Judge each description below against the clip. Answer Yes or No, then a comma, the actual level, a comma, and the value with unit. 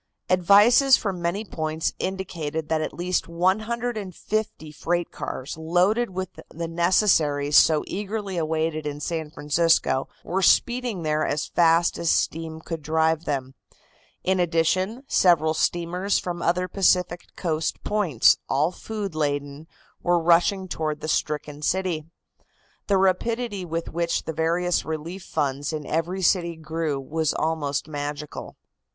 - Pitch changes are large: No, average, 3.2 semitones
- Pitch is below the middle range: No, medium, 165 Hz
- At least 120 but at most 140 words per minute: Yes, slow, 135 wpm